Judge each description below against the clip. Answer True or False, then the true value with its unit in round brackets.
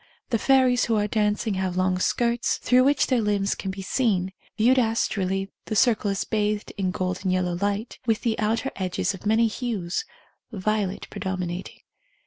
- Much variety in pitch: False (3.3 semitones)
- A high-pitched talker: True (210 Hz)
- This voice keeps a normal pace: True (165 wpm)